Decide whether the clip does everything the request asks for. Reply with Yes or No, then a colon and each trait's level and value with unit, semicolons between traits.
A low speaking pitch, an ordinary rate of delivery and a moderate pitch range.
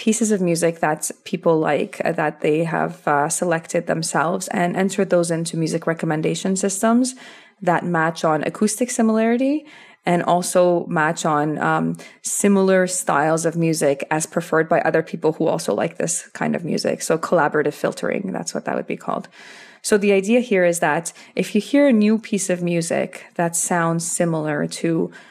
No: medium, 175 Hz; average, 170 wpm; average, 3.9 semitones